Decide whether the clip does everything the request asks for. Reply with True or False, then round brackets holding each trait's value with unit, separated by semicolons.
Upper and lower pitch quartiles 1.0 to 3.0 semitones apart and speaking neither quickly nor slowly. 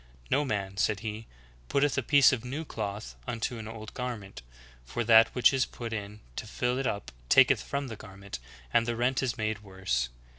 False (3.5 semitones; 195 wpm)